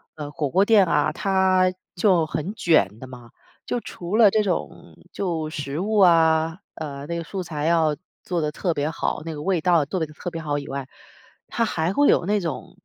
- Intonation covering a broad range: No, average, 3.7 semitones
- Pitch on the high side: No, medium, 165 Hz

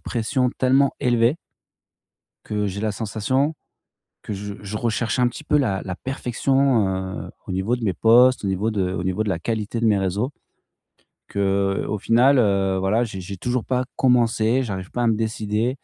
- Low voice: Yes, low, 110 Hz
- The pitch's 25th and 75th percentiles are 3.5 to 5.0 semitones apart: Yes, average, 4.0 semitones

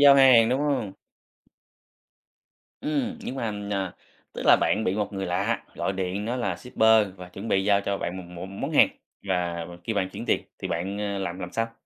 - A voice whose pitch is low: Yes, low, 100 Hz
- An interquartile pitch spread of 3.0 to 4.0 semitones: Yes, average, 3.4 semitones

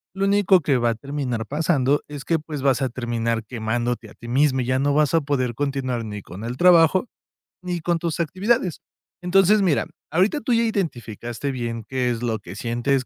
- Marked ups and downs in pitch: Yes, wide, 6.0 semitones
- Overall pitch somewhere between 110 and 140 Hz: Yes, low, 135 Hz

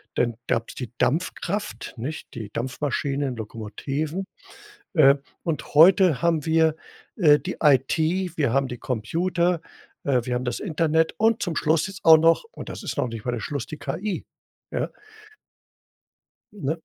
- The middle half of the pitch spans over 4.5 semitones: Yes, average, 5.0 semitones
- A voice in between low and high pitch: Yes, medium, 150 Hz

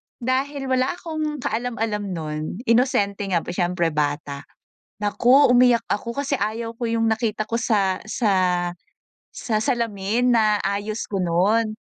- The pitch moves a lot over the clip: No, average, 3.7 semitones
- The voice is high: Yes, high, 225 Hz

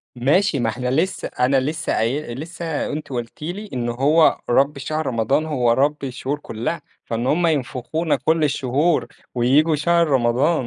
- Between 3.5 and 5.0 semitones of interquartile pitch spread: Yes, average, 4.1 semitones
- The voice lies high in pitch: No, medium, 145 Hz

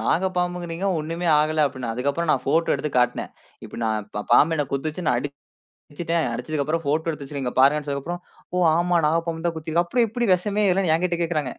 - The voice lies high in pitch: No, medium, 160 Hz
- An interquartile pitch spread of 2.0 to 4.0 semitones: Yes, average, 3.3 semitones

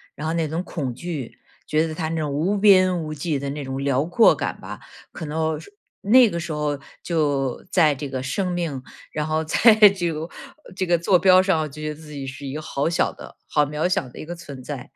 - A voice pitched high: No, medium, 155 Hz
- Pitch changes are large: No, average, 3.4 semitones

